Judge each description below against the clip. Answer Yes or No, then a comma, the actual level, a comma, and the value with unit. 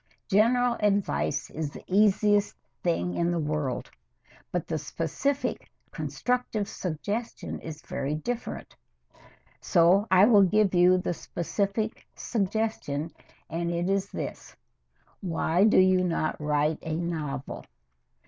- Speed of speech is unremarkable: No, slow, 120 wpm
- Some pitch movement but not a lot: Yes, average, 4.6 semitones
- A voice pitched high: No, medium, 180 Hz